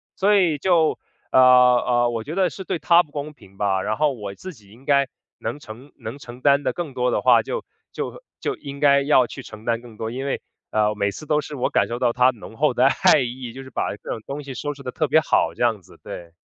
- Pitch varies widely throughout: No, average, 4.0 semitones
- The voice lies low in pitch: Yes, low, 130 Hz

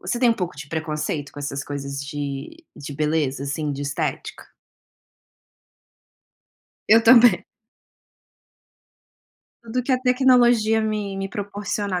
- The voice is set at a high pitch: Yes, high, 195 Hz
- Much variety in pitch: Yes, wide, 8.1 semitones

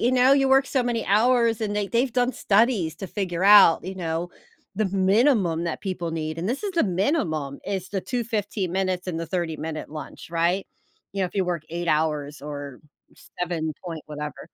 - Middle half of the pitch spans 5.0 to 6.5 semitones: Yes, wide, 5.4 semitones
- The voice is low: No, medium, 185 Hz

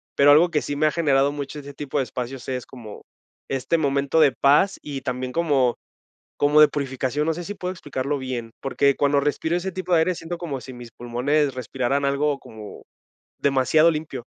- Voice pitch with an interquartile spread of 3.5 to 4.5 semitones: No, average, 2.9 semitones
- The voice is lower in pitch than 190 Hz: Yes, medium, 140 Hz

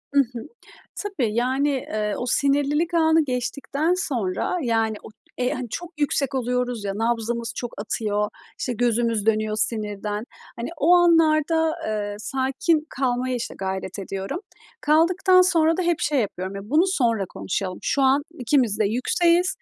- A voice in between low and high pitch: No, very high, 250 Hz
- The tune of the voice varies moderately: No, wide, 6.2 semitones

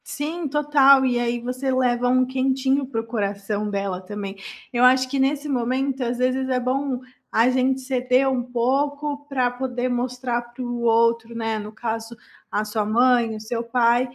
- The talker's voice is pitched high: Yes, very high, 250 Hz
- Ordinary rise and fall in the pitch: No, narrow, 2.2 semitones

